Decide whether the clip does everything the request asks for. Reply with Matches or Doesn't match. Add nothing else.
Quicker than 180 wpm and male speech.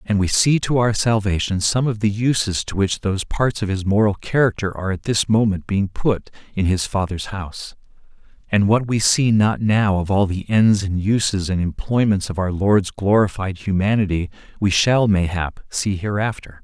Matches